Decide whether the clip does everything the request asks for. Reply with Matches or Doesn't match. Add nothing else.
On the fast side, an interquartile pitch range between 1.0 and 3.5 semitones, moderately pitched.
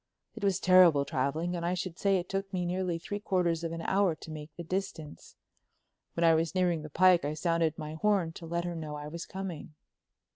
Matches